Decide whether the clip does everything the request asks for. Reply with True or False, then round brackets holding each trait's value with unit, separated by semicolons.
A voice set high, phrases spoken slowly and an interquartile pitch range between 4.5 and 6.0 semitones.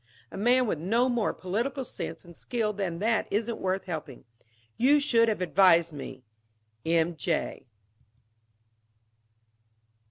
True (200 Hz; 125 wpm; 5.6 semitones)